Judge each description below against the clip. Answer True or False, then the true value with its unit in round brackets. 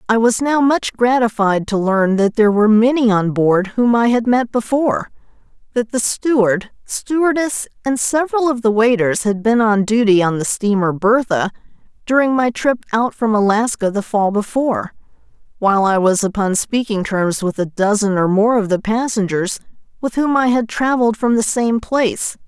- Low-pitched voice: False (225 Hz)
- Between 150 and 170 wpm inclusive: False (180 wpm)